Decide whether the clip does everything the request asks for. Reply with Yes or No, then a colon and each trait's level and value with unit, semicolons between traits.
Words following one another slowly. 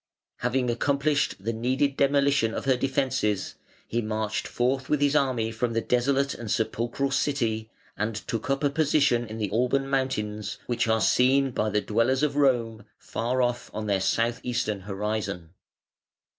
No: average, 160 wpm